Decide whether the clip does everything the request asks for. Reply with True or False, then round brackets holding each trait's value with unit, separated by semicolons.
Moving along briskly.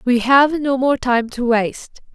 False (195 wpm)